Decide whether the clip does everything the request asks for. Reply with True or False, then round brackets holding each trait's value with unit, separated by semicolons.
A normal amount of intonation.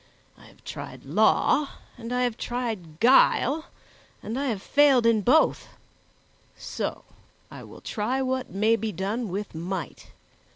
True (4.0 semitones)